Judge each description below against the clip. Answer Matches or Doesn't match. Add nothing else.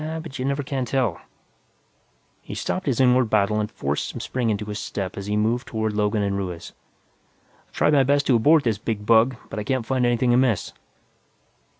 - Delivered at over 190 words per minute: Matches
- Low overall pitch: Matches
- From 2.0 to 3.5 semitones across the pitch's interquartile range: Doesn't match